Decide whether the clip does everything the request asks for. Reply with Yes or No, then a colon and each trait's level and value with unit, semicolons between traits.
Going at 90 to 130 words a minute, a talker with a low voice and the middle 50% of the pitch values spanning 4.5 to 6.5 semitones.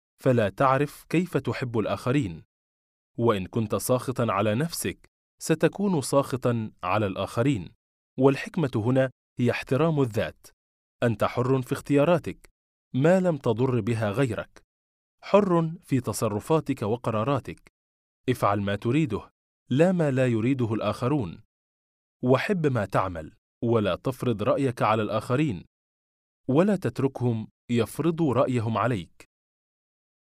Yes: average, 105 wpm; low, 120 Hz; average, 5.1 semitones